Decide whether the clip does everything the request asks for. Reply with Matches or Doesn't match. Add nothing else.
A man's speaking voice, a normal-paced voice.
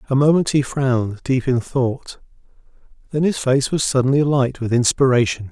Matches